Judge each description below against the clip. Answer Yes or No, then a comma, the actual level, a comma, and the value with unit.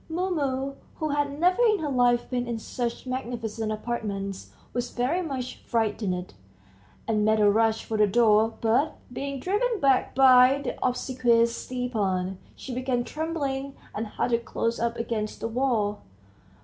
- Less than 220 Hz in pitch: No, high, 245 Hz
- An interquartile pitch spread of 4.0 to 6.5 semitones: No, average, 3.6 semitones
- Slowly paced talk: No, average, 150 wpm